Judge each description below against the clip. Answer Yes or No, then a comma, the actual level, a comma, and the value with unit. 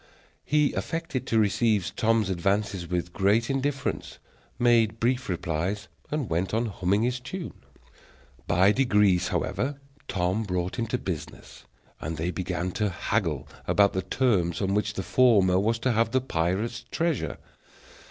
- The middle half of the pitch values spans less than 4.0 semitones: No, average, 4.7 semitones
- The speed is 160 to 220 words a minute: No, average, 145 wpm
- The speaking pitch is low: Yes, low, 105 Hz